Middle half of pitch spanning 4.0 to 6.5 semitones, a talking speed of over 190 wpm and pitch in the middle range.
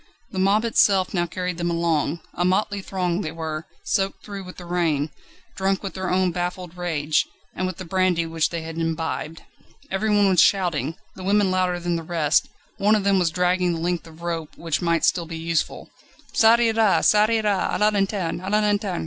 No: average, 2.8 semitones; average, 200 wpm; medium, 180 Hz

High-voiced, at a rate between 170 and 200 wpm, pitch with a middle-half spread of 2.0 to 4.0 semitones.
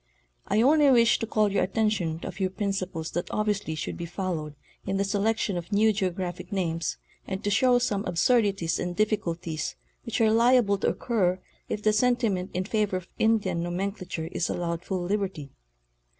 Yes: high, 195 Hz; average, 180 wpm; average, 3.5 semitones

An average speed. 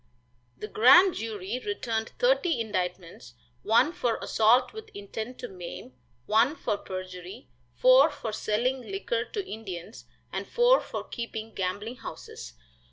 No: slow, 130 wpm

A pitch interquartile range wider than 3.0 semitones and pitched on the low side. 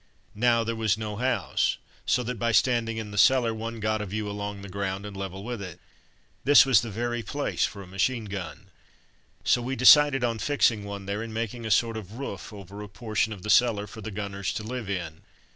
No: average, 2.7 semitones; low, 110 Hz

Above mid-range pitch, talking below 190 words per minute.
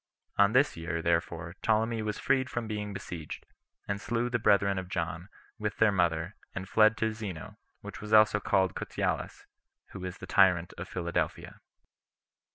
No: low, 100 Hz; average, 160 wpm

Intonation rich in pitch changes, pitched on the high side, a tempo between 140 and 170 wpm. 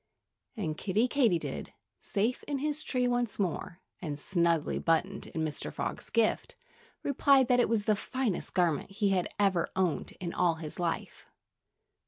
Yes: wide, 6.1 semitones; high, 195 Hz; average, 155 wpm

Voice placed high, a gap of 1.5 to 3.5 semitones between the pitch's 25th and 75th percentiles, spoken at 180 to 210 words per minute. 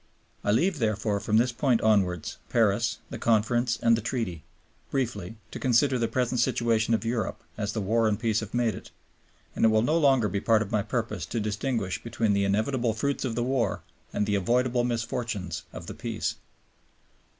No: low, 115 Hz; narrow, 2.5 semitones; average, 190 wpm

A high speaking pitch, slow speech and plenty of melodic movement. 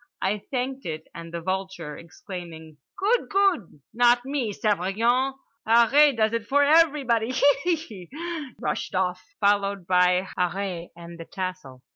Yes: high, 205 Hz; slow, 130 wpm; wide, 6.9 semitones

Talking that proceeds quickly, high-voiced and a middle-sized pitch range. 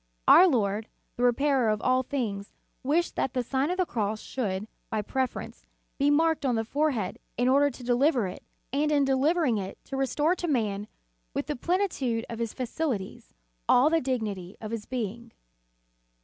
No: average, 175 wpm; very high, 250 Hz; average, 4.7 semitones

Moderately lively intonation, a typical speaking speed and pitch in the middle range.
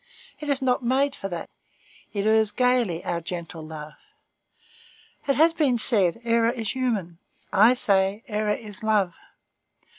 No: average, 4.7 semitones; average, 145 wpm; high, 220 Hz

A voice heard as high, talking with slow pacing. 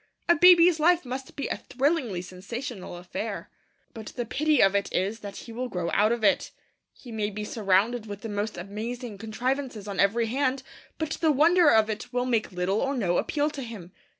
No: high, 230 Hz; average, 200 wpm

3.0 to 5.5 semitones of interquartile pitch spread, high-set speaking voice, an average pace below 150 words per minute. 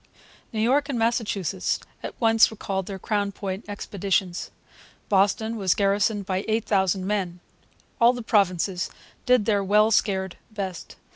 No: narrow, 2.6 semitones; high, 205 Hz; slow, 135 wpm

